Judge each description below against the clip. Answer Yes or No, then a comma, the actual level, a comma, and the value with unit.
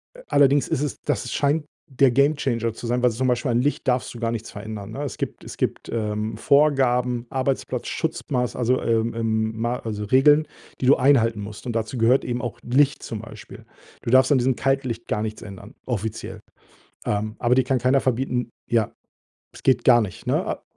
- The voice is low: Yes, low, 120 Hz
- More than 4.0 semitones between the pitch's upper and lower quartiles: No, average, 2.9 semitones